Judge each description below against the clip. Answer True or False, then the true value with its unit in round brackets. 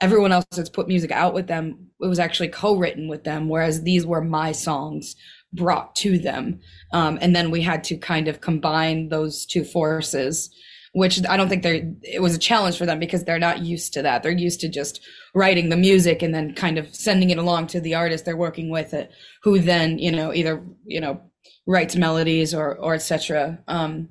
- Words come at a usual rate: False (215 wpm)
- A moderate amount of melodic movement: False (1.8 semitones)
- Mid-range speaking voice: True (165 Hz)